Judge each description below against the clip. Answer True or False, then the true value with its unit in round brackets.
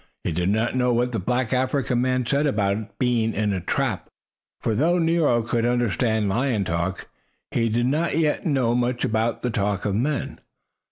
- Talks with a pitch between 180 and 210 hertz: False (120 Hz)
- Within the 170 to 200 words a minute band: True (180 wpm)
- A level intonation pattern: False (3.1 semitones)